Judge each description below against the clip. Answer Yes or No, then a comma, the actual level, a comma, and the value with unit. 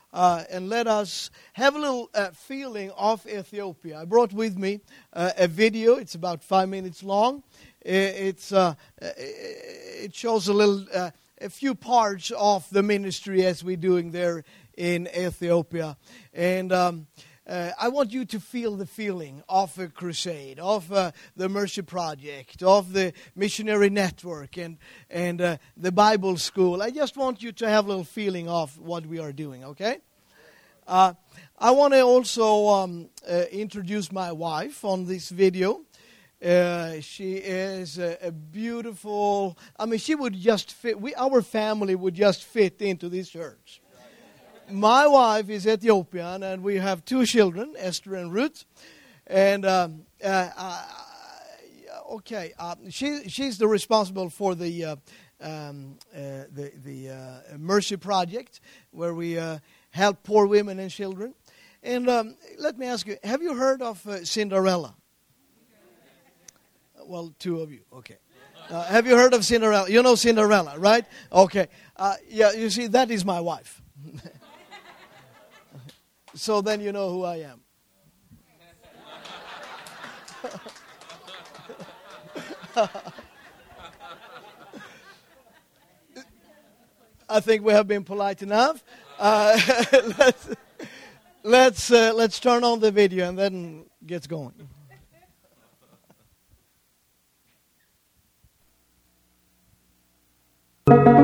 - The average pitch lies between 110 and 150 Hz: No, high, 195 Hz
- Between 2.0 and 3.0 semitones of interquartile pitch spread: No, average, 4.0 semitones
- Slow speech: Yes, slow, 130 wpm